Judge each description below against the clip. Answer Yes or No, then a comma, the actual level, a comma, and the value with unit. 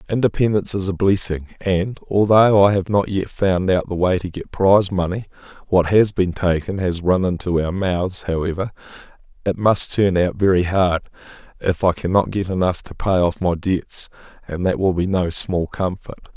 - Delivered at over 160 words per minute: Yes, average, 180 wpm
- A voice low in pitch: Yes, very low, 95 Hz